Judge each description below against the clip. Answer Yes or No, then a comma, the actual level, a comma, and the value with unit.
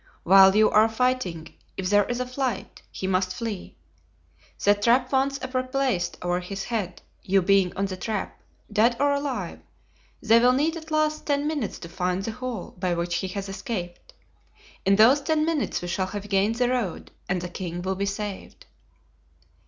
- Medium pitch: No, high, 205 Hz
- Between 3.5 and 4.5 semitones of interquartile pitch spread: No, average, 5.3 semitones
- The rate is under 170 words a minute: No, average, 180 wpm